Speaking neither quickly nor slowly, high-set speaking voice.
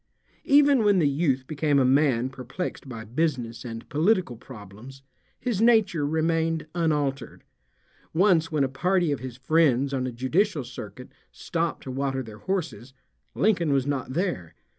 No: average, 150 wpm; medium, 145 Hz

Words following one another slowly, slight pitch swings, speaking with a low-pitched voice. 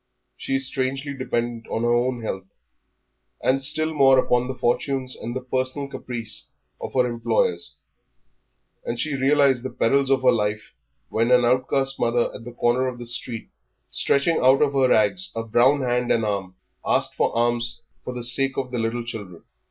No: average, 175 wpm; narrow, 2.3 semitones; low, 125 Hz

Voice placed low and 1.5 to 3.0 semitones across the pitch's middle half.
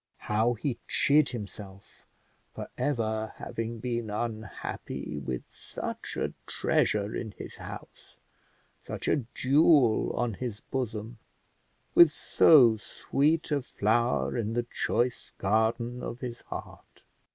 Yes: low, 115 Hz; average, 2.7 semitones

